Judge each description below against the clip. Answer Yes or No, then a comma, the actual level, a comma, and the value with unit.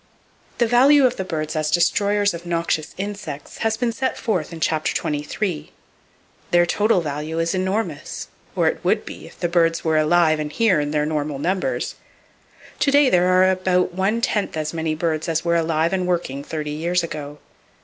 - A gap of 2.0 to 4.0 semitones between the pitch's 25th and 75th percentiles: Yes, average, 3.7 semitones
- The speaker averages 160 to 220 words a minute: Yes, average, 180 wpm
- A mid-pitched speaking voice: Yes, medium, 170 Hz